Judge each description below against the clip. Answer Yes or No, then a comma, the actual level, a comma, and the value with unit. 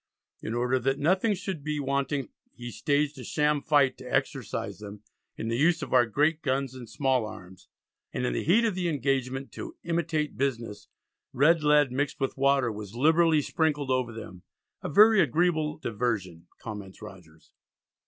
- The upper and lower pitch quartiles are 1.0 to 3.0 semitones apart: No, average, 4.6 semitones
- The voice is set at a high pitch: No, low, 135 Hz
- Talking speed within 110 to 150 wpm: No, average, 170 wpm